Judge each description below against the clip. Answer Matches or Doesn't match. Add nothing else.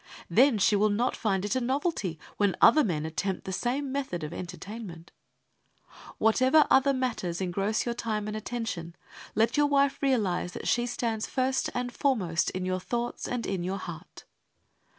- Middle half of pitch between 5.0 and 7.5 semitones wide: Matches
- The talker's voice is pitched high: Matches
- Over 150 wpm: Matches